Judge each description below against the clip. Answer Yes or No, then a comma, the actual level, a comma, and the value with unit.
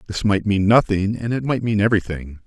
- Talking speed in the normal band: No, fast, 220 wpm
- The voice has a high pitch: No, low, 105 Hz